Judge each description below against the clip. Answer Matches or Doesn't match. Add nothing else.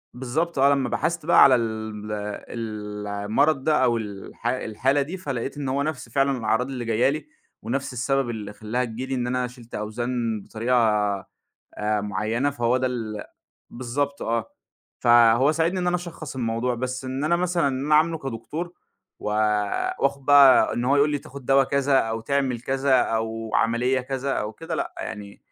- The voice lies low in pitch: Matches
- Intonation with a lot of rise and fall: Doesn't match